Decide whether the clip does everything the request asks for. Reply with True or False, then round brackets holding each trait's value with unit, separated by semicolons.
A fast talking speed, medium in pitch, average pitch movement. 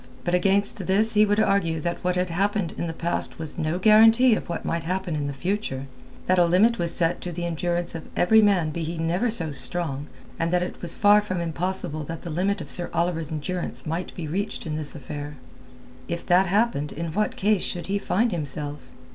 True (215 wpm; 175 Hz; 3.4 semitones)